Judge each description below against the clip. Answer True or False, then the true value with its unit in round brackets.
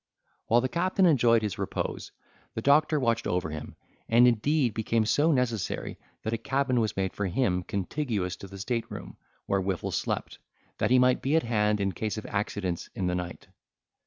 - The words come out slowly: False (190 wpm)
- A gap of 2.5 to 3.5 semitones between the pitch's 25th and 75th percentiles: False (4.7 semitones)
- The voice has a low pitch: True (110 Hz)